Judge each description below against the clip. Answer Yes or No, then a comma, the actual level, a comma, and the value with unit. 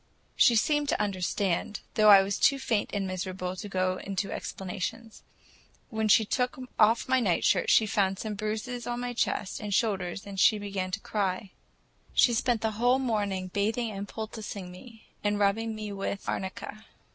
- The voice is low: No, high, 210 Hz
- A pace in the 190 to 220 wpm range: No, average, 170 wpm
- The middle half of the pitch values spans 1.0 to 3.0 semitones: Yes, narrow, 2.6 semitones